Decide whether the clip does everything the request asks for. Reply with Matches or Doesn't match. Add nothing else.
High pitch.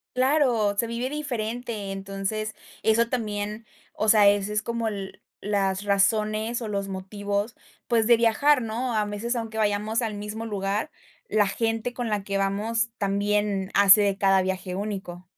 Matches